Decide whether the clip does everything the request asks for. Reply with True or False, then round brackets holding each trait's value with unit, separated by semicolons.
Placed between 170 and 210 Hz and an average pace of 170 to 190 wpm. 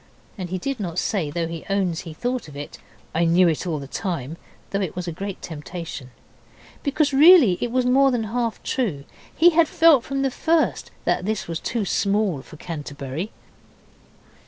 True (190 Hz; 185 wpm)